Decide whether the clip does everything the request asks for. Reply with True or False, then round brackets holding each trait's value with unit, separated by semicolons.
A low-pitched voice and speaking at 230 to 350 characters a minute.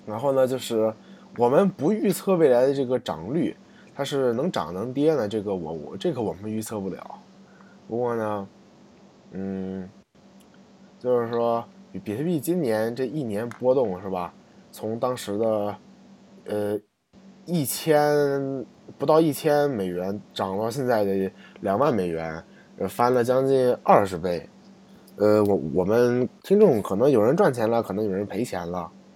False (120 Hz; 215 characters per minute)